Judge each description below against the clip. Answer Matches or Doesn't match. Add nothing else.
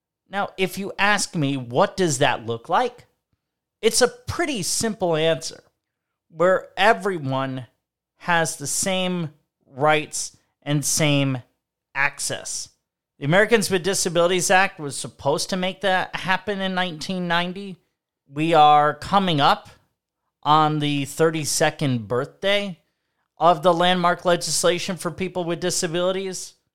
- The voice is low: Doesn't match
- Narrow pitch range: Doesn't match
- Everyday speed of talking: Doesn't match